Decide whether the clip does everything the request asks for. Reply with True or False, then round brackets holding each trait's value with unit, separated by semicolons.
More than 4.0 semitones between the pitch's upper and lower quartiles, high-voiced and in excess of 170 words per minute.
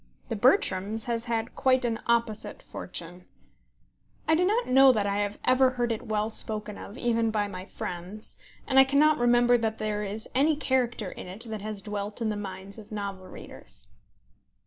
False (3.1 semitones; 220 Hz; 185 wpm)